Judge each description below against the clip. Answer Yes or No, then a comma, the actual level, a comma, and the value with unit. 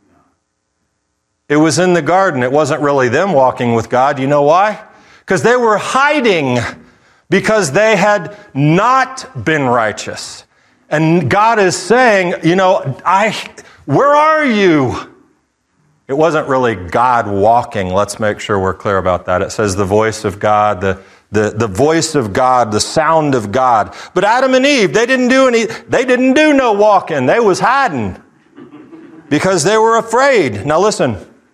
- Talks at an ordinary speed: Yes, average, 160 wpm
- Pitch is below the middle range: No, medium, 160 Hz